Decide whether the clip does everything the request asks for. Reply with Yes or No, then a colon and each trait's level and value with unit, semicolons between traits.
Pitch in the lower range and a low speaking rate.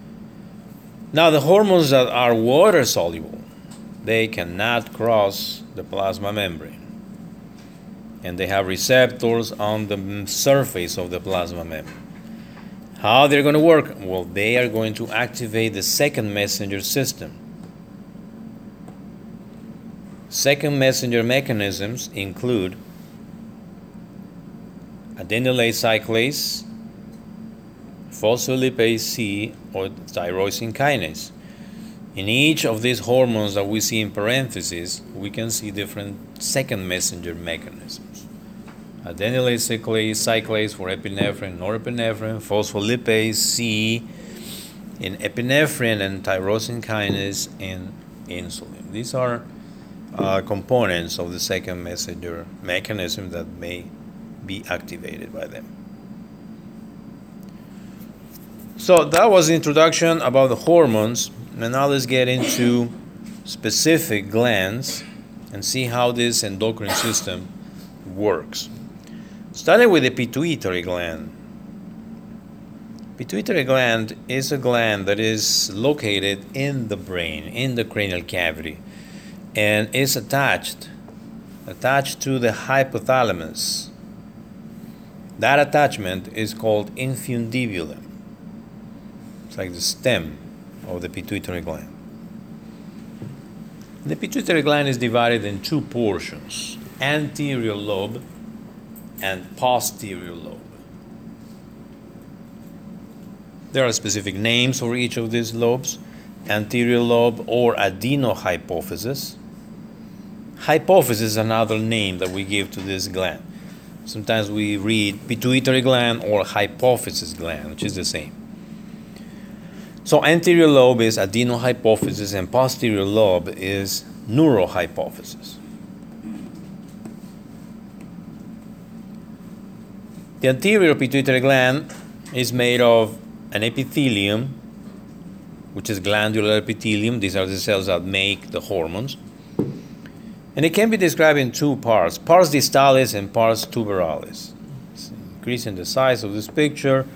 Yes: low, 125 Hz; slow, 105 wpm